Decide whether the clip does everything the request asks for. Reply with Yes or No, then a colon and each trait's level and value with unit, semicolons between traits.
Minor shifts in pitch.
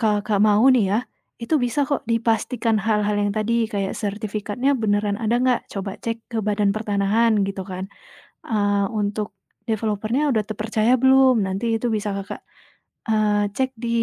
Yes: narrow, 2.2 semitones